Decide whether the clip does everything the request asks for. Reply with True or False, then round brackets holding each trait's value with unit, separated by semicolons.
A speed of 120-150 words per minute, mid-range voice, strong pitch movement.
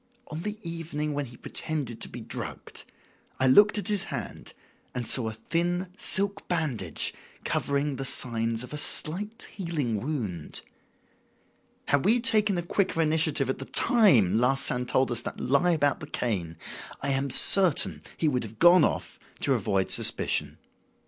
False (160 wpm; 145 Hz; 6.1 semitones)